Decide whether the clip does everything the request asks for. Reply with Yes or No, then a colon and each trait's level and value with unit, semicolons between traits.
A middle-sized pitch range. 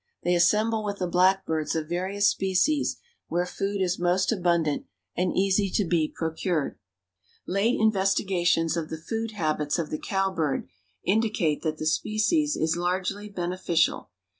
Yes: average, 3.4 semitones